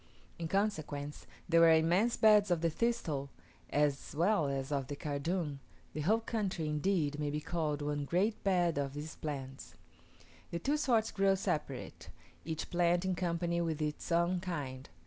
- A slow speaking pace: No, average, 165 wpm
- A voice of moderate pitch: Yes, medium, 165 Hz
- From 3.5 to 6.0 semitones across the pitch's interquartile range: Yes, average, 4.2 semitones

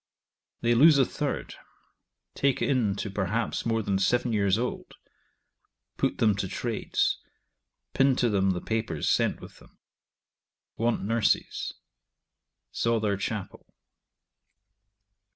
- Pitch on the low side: Yes, low, 110 Hz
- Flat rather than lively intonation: No, average, 3.1 semitones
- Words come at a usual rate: No, slow, 115 wpm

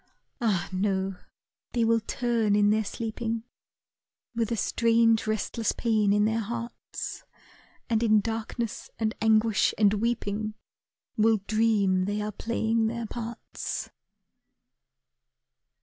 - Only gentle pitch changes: Yes, narrow, 1.6 semitones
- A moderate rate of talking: No, slow, 115 wpm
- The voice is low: No, high, 220 Hz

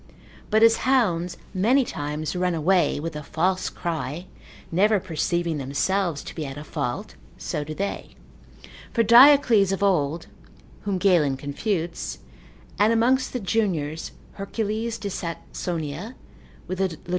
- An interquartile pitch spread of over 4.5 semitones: Yes, average, 5.2 semitones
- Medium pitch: Yes, medium, 180 Hz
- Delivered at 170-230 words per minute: No, slow, 135 wpm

